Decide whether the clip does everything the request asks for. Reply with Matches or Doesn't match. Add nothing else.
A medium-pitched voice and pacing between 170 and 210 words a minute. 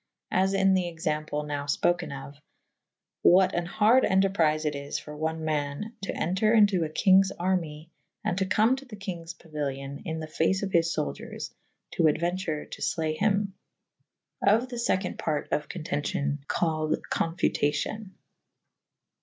Doesn't match